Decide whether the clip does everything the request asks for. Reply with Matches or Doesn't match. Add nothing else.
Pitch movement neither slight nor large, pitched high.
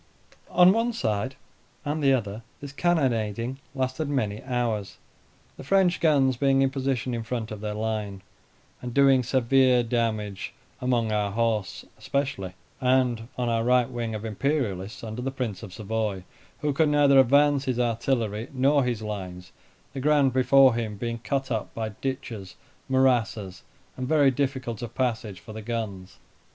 Doesn't match